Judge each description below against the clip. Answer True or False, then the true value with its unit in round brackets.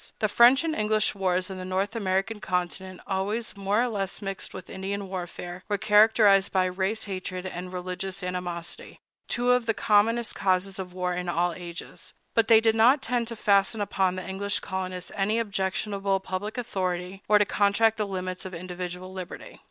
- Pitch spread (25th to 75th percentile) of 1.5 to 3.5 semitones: True (2.5 semitones)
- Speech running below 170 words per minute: False (175 wpm)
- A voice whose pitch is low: False (195 Hz)